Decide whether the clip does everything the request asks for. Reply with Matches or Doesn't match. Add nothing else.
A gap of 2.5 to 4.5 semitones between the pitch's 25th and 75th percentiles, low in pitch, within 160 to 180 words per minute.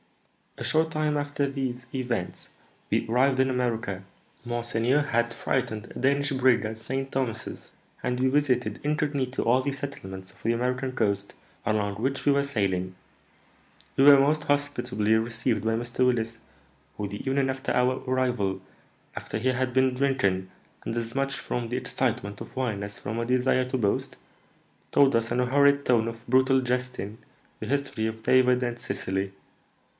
Matches